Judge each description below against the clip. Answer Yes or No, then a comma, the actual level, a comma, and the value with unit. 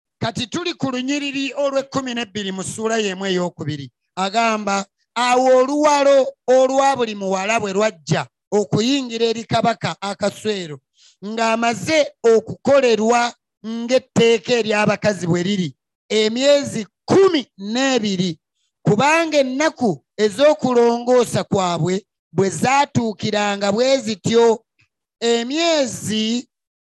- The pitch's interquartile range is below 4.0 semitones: No, average, 4.6 semitones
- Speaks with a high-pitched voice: Yes, high, 230 Hz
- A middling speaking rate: No, slow, 85 wpm